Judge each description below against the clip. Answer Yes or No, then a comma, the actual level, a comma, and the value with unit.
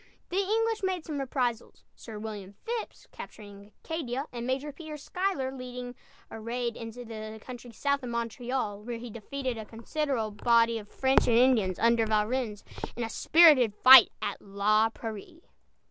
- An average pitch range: Yes, average, 3.7 semitones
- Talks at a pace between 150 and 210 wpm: Yes, average, 160 wpm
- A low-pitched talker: No, high, 240 Hz